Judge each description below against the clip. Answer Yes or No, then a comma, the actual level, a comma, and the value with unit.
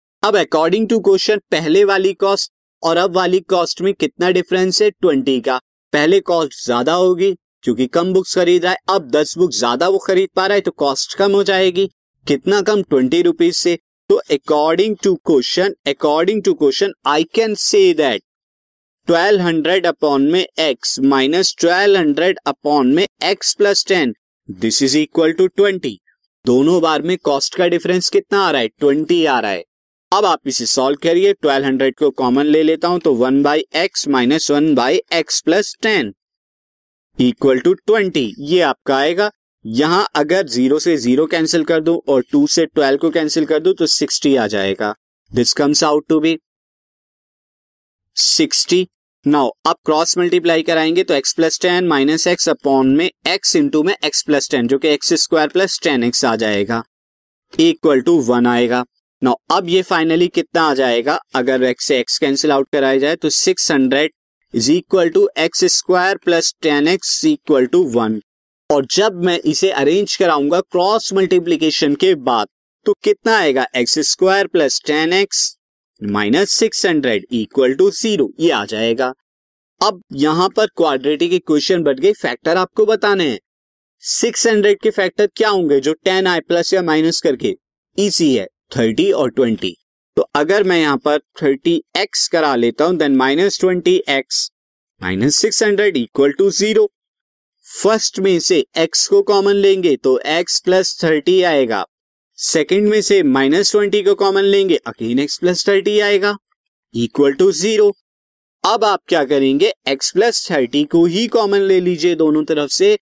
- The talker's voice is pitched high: No, medium, 170 Hz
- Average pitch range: No, wide, 5.7 semitones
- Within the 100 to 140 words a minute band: No, average, 155 wpm